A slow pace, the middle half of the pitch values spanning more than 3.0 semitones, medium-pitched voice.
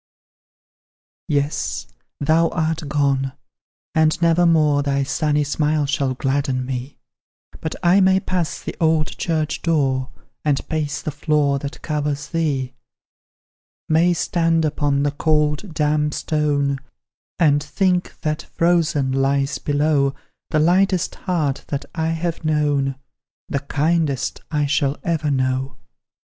No: slow, 125 wpm; narrow, 2.4 semitones; medium, 150 Hz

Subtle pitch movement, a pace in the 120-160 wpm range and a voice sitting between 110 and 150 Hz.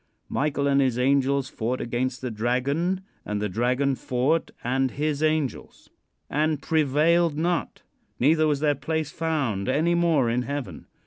No: average, 3.7 semitones; average, 145 wpm; medium, 140 Hz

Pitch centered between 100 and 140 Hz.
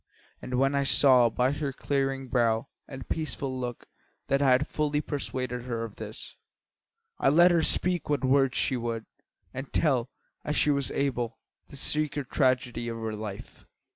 Yes: low, 135 Hz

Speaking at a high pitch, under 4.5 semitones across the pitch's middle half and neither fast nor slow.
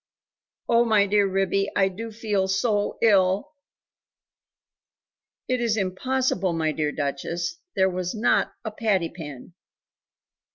No: high, 195 Hz; average, 3.4 semitones; slow, 120 wpm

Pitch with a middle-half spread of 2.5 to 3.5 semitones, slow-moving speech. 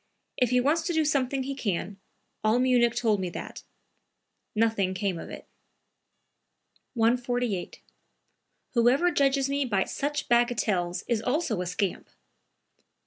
No: average, 4.7 semitones; slow, 130 wpm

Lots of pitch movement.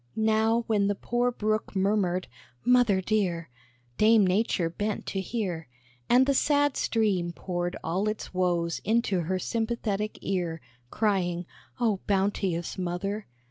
No: average, 3.6 semitones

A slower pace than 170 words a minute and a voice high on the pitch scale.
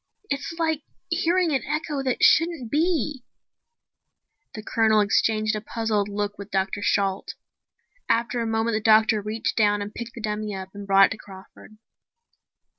Yes: average, 160 wpm; high, 220 Hz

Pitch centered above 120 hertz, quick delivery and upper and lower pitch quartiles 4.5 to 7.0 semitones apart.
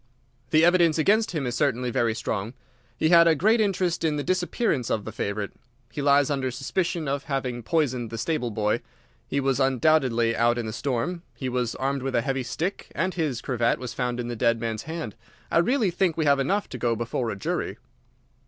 Yes: low, 135 Hz; fast, 210 wpm; wide, 5.5 semitones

